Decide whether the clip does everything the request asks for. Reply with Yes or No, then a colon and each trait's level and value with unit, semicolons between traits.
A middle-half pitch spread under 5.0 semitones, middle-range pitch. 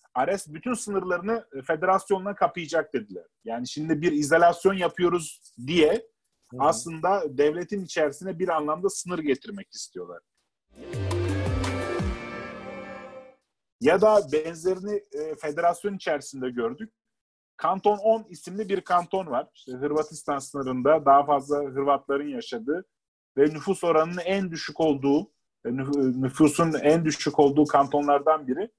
No: average, 5.3 semitones; medium, 165 Hz